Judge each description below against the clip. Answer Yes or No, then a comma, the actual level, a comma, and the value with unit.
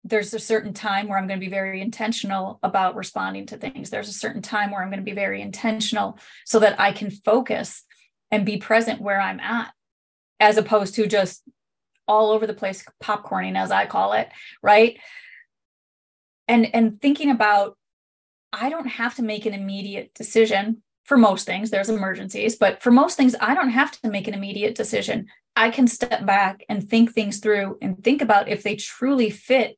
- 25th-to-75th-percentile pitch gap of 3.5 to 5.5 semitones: No, narrow, 2.5 semitones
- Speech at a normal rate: Yes, average, 190 wpm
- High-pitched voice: Yes, high, 215 Hz